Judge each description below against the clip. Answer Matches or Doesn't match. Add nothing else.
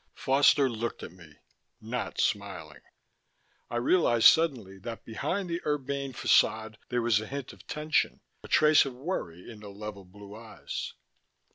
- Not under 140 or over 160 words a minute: Matches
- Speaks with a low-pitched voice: Matches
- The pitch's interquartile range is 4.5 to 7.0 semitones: Matches